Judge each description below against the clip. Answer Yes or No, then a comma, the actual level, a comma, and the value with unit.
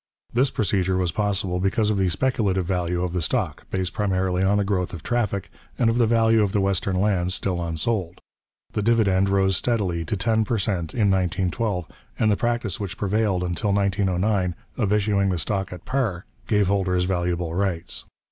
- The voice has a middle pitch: No, very low, 95 Hz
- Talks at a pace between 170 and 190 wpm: Yes, average, 185 wpm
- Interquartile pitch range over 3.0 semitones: No, average, 2.7 semitones